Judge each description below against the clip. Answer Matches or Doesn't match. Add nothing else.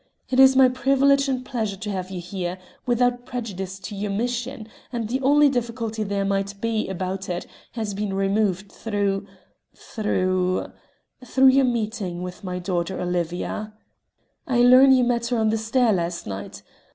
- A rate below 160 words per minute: Doesn't match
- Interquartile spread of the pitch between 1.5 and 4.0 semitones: Doesn't match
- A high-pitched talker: Matches